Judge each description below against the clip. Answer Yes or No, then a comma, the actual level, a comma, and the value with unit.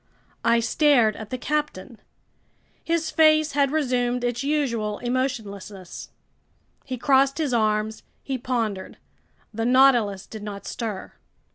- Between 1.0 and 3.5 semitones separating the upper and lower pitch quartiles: No, average, 4.3 semitones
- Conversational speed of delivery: No, slow, 120 wpm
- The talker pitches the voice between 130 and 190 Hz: No, high, 245 Hz